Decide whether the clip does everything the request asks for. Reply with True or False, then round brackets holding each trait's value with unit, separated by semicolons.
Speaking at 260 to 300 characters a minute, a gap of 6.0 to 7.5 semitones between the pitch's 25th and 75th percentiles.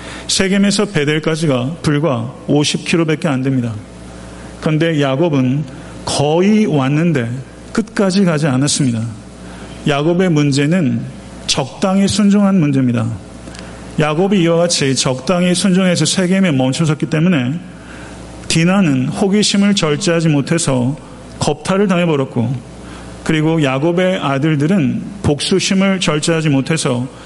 False (275 characters per minute; 5.4 semitones)